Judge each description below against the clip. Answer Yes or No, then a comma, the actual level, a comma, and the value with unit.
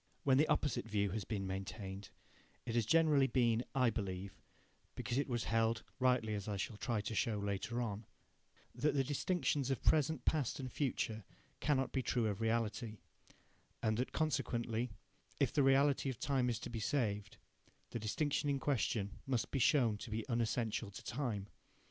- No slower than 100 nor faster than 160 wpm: No, average, 175 wpm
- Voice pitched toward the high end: No, low, 115 Hz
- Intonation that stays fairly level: No, average, 4.0 semitones